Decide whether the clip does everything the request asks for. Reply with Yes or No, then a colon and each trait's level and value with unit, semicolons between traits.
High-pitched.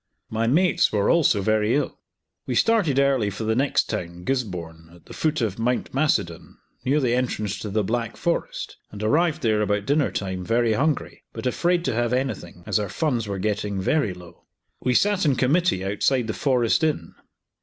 No: low, 115 Hz